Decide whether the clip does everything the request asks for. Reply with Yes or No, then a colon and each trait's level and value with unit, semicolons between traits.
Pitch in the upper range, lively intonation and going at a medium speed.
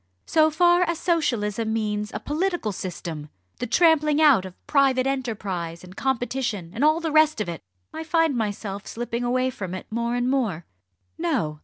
Yes: high, 245 Hz; wide, 7.0 semitones; average, 170 wpm